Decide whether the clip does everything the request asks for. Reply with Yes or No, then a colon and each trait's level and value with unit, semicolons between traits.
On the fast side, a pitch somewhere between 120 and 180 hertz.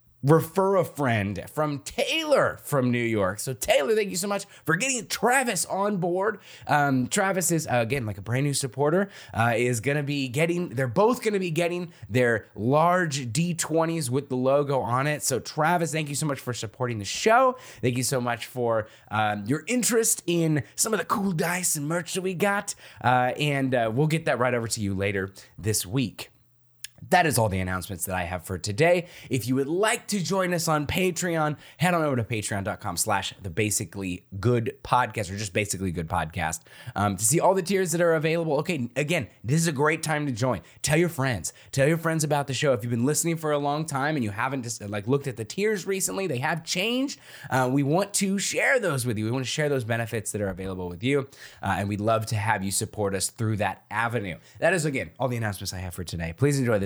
Yes: fast, 230 wpm; low, 135 Hz